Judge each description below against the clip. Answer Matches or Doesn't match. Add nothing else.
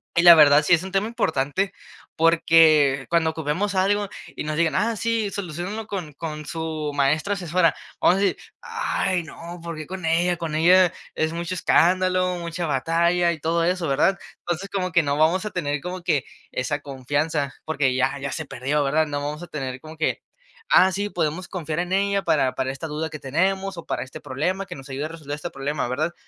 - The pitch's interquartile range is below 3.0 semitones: Doesn't match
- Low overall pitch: Doesn't match